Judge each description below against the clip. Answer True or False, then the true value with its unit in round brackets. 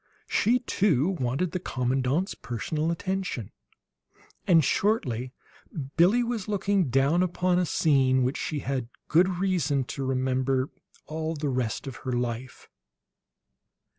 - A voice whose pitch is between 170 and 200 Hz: False (150 Hz)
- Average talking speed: False (125 wpm)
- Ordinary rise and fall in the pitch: False (5.9 semitones)